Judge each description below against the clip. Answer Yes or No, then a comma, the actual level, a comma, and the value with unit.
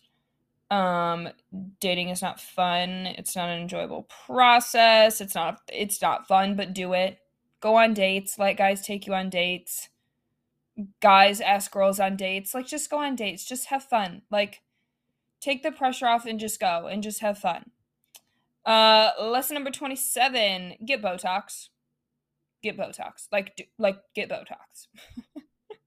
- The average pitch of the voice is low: No, high, 200 Hz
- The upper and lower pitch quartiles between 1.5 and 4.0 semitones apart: Yes, average, 3.5 semitones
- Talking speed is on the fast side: No, average, 150 wpm